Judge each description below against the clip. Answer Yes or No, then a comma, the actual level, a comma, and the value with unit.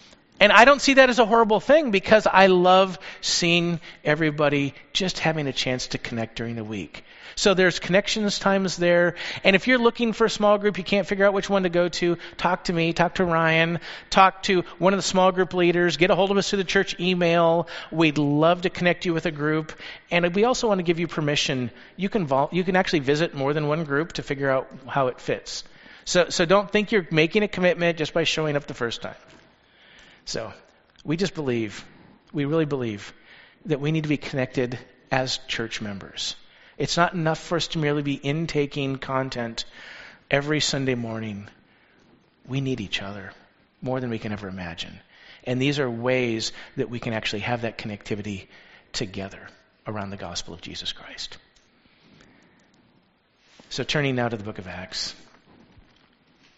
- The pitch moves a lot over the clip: Yes, wide, 6.4 semitones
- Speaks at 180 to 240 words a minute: Yes, average, 190 wpm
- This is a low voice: No, medium, 155 Hz